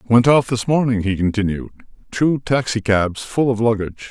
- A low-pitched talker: Yes, low, 115 Hz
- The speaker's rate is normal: Yes, average, 175 wpm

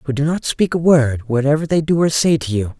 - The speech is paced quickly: Yes, fast, 280 wpm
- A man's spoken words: Yes, male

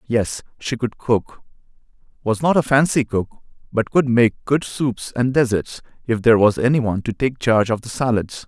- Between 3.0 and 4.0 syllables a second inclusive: No, 4.9 syllables/s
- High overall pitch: No, low, 120 Hz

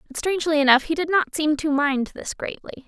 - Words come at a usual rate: No, fast, 230 wpm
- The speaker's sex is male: No, female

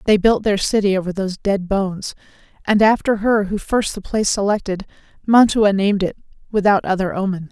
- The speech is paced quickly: No, average, 175 wpm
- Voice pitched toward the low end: No, high, 200 Hz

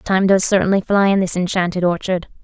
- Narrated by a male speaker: No, female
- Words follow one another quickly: No, average, 195 wpm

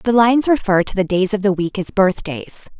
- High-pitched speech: Yes, high, 200 Hz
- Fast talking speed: Yes, fast, 235 wpm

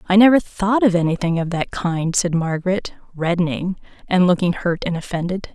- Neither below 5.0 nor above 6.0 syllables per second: Yes, 5.4 syllables/s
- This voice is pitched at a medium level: Yes, medium, 180 Hz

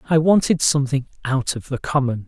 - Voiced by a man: Yes, male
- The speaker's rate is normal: Yes, average, 185 wpm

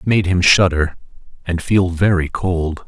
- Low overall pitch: Yes, very low, 90 Hz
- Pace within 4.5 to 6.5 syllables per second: No, 4.3 syllables/s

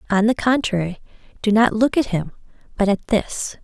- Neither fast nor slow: Yes, average, 180 wpm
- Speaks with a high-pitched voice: Yes, high, 215 Hz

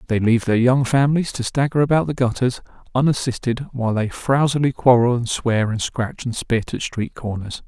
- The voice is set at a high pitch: No, low, 125 Hz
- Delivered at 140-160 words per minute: No, average, 190 wpm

